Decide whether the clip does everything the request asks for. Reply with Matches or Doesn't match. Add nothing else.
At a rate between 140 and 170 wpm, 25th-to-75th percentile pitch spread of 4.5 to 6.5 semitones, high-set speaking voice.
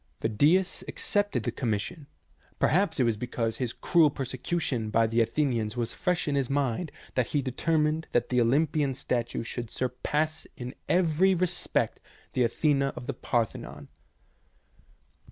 Doesn't match